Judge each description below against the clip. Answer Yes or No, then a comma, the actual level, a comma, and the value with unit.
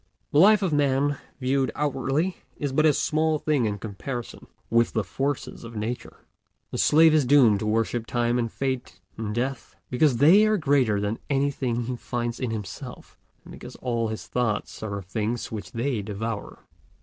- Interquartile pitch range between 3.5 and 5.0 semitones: Yes, average, 4.2 semitones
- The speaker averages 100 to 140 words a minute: No, average, 175 wpm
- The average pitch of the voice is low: Yes, low, 125 Hz